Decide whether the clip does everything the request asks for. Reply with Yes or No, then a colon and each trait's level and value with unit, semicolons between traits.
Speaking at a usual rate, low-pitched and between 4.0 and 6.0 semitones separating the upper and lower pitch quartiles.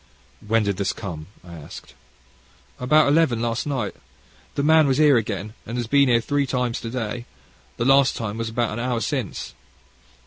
No: average, 180 wpm; low, 120 Hz; average, 3.6 semitones